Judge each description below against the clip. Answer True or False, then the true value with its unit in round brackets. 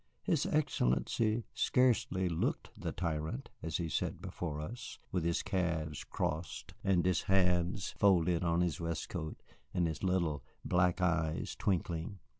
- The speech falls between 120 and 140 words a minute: True (135 wpm)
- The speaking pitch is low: True (90 Hz)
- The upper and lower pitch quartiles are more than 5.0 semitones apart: False (2.9 semitones)